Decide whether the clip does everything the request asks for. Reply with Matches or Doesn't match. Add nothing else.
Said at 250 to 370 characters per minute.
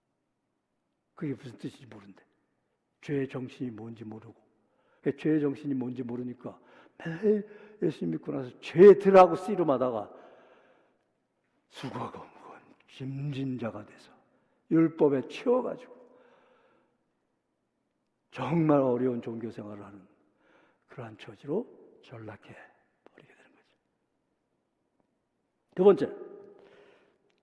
Doesn't match